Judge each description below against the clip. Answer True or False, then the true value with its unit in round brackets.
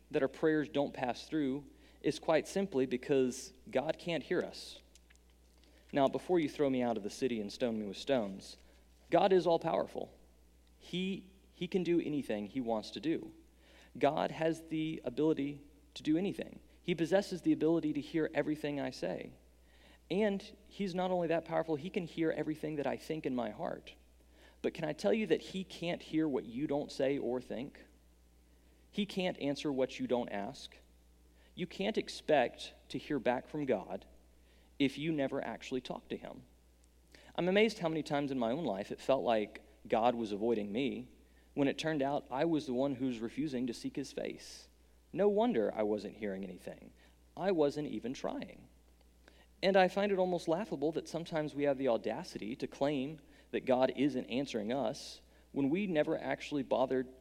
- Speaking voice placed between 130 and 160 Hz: True (135 Hz)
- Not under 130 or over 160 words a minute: False (180 wpm)